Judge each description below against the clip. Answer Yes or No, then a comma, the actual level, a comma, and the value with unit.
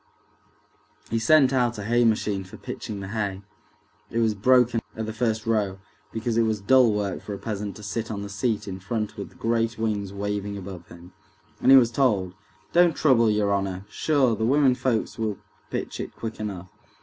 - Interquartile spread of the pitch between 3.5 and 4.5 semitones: No, average, 2.7 semitones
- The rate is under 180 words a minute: No, average, 190 wpm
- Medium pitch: No, low, 110 Hz